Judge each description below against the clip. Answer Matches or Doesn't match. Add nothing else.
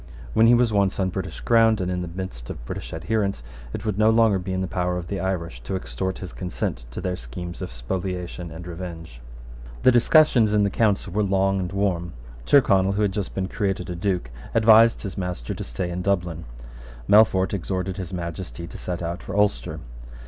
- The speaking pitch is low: Matches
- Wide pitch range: Doesn't match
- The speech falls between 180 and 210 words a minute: Matches